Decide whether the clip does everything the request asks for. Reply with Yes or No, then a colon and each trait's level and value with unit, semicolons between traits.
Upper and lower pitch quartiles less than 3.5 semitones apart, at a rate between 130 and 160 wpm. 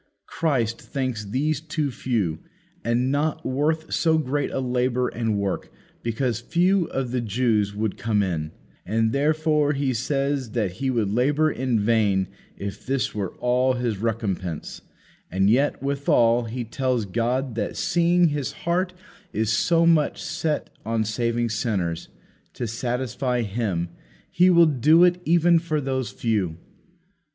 No: average, 4.8 semitones; average, 145 wpm